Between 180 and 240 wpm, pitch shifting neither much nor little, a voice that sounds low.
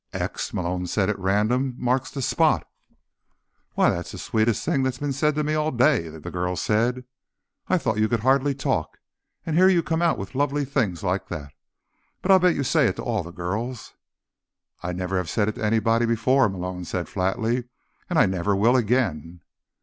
No: average, 195 wpm; wide, 6.3 semitones; low, 115 Hz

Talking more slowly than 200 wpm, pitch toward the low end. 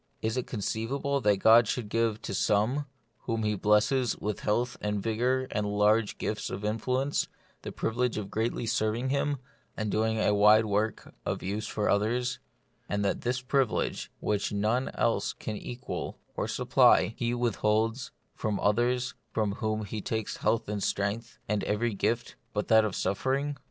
Yes: average, 165 wpm; low, 110 Hz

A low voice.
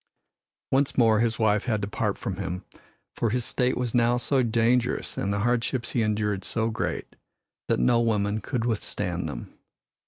Yes: low, 115 Hz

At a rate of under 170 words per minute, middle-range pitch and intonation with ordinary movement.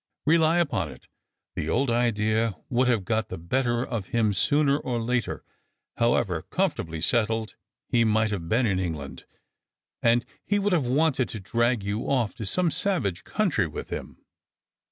No: average, 160 wpm; low, 115 Hz; average, 4.6 semitones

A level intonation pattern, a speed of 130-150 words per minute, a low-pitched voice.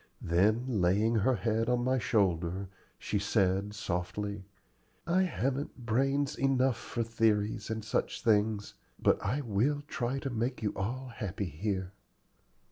No: average, 4.2 semitones; slow, 135 wpm; low, 110 Hz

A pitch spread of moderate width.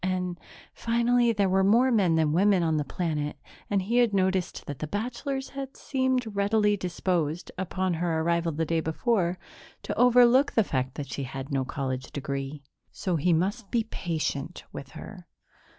No: wide, 6.0 semitones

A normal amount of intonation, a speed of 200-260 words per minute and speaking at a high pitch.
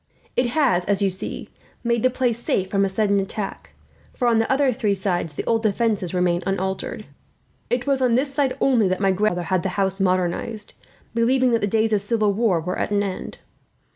Yes: average, 3.8 semitones; fast, 205 wpm; high, 205 Hz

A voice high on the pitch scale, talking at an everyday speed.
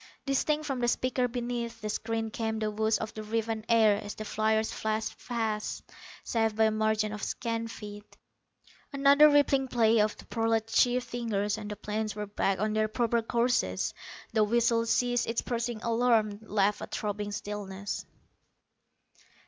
Yes: high, 220 Hz; average, 165 wpm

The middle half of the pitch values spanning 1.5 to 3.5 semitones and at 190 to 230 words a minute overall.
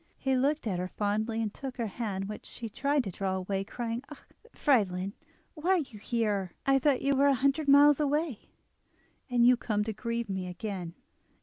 No: wide, 5.4 semitones; average, 195 wpm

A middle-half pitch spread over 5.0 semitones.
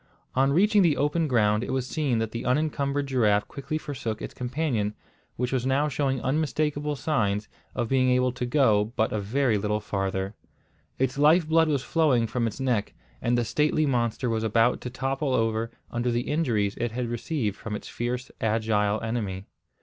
No: average, 4.2 semitones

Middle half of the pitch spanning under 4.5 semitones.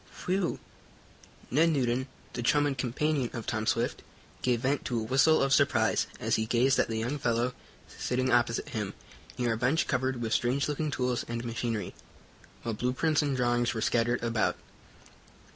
Yes: average, 2.7 semitones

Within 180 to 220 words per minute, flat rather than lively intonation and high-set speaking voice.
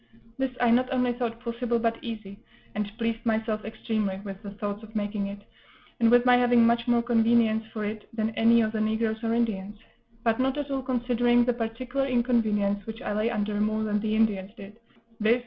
Yes: average, 200 wpm; narrow, 2.1 semitones; high, 225 Hz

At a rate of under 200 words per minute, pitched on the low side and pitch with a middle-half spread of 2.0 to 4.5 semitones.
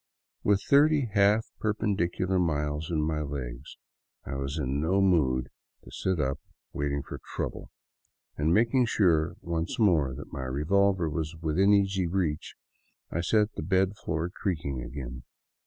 No: average, 145 wpm; very low, 85 Hz; average, 5.2 semitones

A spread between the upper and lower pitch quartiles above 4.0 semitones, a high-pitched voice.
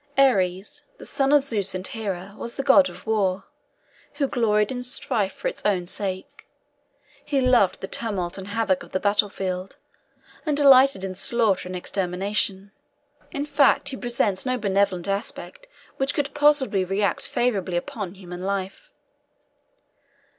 Yes: average, 5.1 semitones; high, 205 Hz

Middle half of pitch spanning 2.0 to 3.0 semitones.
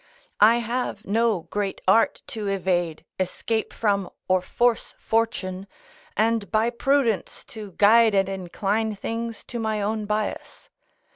Yes: average, 2.7 semitones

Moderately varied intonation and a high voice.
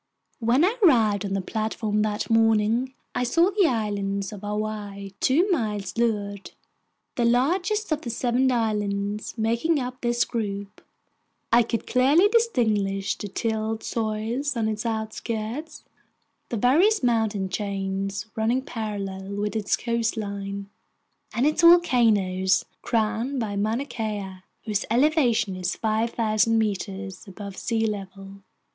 Yes: average, 3.2 semitones; high, 220 Hz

